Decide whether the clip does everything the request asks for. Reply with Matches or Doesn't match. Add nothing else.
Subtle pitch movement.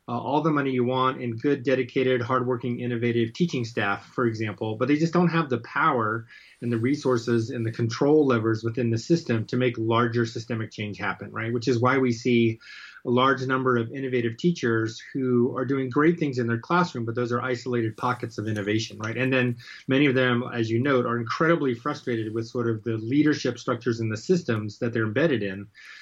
Matches